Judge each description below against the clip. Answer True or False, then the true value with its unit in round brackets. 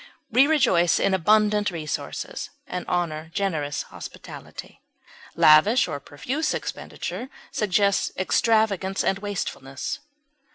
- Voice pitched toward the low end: False (195 Hz)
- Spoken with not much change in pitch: False (4.9 semitones)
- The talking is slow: True (95 wpm)